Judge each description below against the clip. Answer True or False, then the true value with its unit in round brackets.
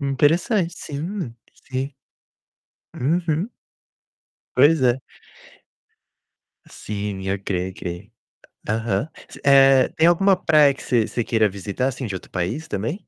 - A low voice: True (130 Hz)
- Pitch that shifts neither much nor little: False (6.9 semitones)